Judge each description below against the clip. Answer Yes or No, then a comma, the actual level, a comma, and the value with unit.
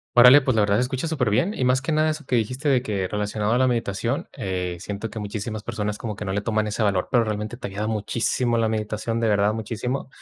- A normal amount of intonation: Yes, average, 3.2 semitones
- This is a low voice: Yes, low, 110 Hz